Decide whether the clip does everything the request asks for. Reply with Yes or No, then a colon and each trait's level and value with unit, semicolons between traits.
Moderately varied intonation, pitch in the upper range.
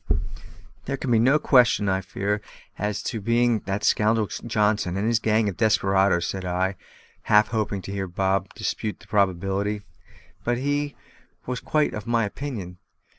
No: average, 3.2 semitones; low, 105 Hz